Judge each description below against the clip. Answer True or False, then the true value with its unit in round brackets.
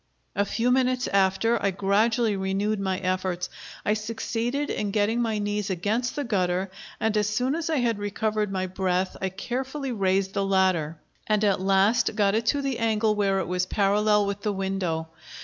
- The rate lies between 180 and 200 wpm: True (185 wpm)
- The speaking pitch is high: True (205 Hz)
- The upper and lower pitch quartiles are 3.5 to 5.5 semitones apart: False (2.9 semitones)